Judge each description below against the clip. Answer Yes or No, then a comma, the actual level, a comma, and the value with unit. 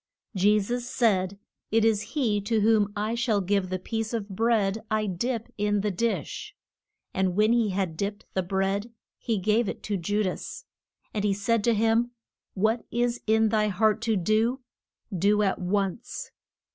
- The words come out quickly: No, average, 170 wpm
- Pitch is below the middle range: No, high, 210 Hz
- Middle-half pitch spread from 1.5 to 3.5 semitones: Yes, narrow, 2.4 semitones